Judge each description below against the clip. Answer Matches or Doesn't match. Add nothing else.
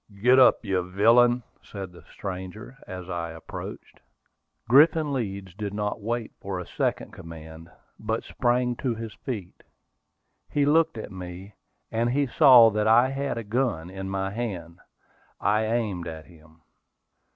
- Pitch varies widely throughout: Doesn't match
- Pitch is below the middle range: Matches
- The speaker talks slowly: Doesn't match